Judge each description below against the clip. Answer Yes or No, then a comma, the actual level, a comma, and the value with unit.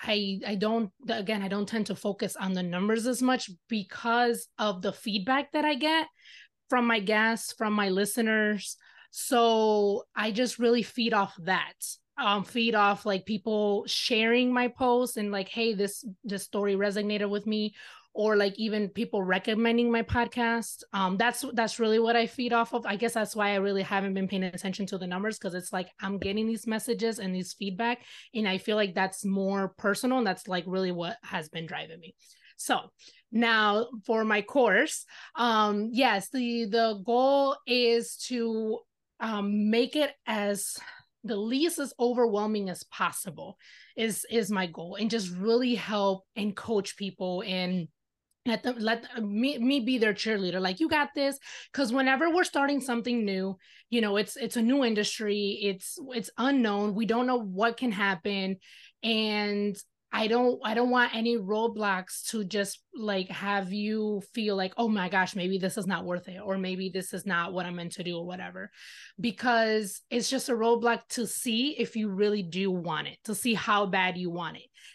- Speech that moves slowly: No, average, 185 wpm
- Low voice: No, high, 215 Hz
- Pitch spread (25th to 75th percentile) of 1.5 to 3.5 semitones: Yes, average, 3.0 semitones